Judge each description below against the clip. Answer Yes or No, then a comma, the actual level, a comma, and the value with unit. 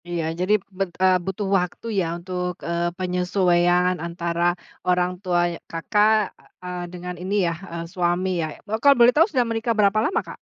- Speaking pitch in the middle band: Yes, medium, 180 Hz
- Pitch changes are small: Yes, narrow, 2.3 semitones